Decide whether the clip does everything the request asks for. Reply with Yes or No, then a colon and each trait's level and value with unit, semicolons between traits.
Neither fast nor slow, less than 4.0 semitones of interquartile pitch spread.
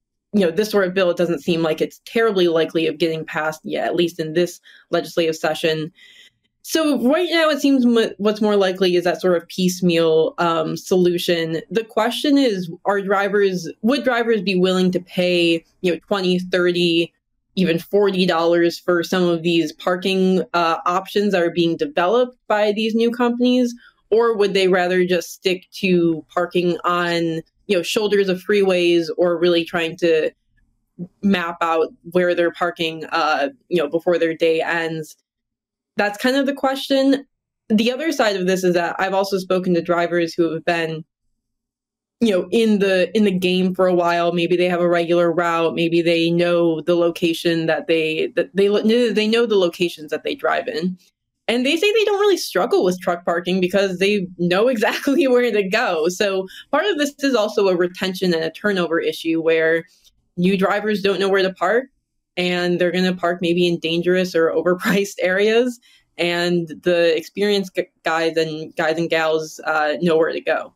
Yes: average, 180 wpm; average, 3.3 semitones